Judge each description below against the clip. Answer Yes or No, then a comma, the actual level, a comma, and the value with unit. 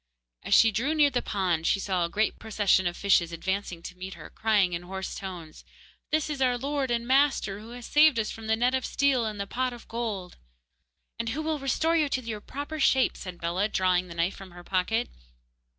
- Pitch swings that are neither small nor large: No, wide, 5.7 semitones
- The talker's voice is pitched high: Yes, high, 220 Hz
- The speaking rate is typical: No, fast, 220 wpm